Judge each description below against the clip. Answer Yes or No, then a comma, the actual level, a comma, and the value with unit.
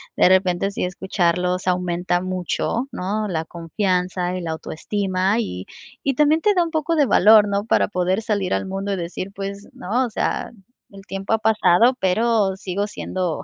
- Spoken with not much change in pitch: No, average, 3.0 semitones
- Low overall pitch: No, high, 195 Hz